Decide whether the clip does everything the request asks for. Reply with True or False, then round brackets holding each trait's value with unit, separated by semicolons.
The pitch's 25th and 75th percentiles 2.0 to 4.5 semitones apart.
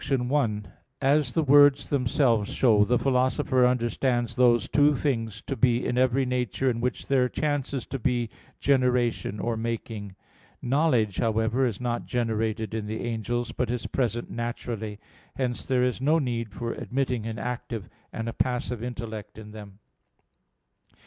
True (2.4 semitones)